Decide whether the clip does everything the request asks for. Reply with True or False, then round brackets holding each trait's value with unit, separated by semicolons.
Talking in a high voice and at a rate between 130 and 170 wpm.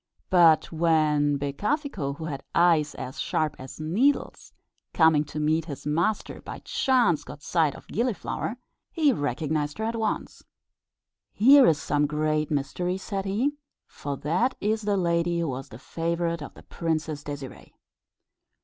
False (160 Hz; 150 wpm)